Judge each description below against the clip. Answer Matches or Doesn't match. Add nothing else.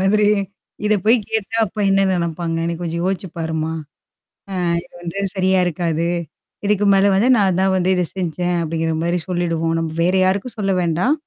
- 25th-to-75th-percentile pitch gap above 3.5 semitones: Doesn't match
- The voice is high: Doesn't match